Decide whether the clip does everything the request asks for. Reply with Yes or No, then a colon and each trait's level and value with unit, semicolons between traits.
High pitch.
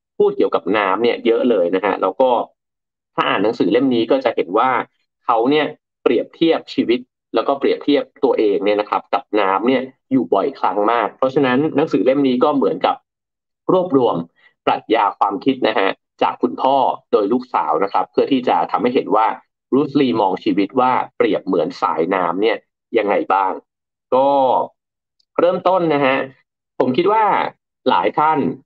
Yes: very high, 310 Hz